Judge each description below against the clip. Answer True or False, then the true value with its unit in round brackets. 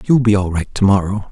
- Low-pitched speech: True (100 Hz)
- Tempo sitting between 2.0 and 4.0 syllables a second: False (6.1 syllables/s)